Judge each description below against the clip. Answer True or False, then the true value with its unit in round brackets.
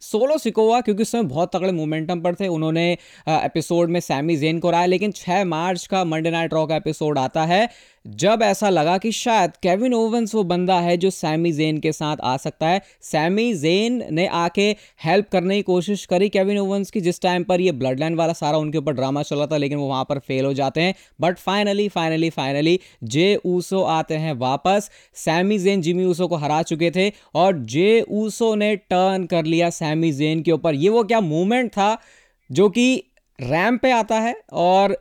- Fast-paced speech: True (205 wpm)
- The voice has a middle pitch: True (180 Hz)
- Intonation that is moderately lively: True (4.1 semitones)